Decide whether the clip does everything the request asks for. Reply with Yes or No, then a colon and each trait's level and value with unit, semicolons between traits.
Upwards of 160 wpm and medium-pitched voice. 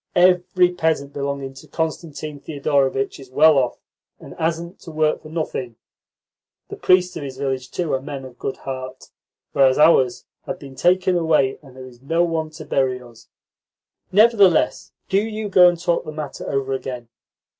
Yes: average, 170 wpm; medium, 150 Hz